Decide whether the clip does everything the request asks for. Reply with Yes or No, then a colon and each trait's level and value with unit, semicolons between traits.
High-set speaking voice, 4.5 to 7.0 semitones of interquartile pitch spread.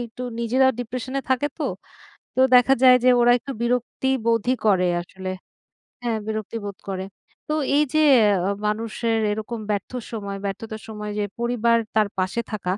No: high, 225 Hz; average, 2.8 semitones